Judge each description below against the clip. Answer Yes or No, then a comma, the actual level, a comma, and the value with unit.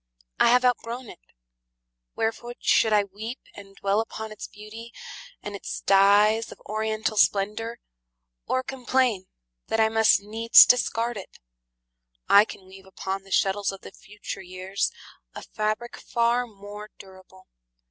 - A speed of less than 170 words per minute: Yes, average, 140 wpm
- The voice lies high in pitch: Yes, high, 215 Hz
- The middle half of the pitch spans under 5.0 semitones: Yes, narrow, 2.6 semitones